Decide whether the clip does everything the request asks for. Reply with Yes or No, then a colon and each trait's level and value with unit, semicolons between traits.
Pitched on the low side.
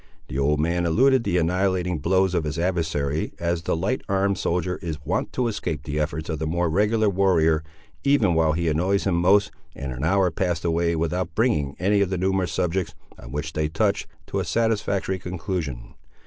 Yes: very low, 85 Hz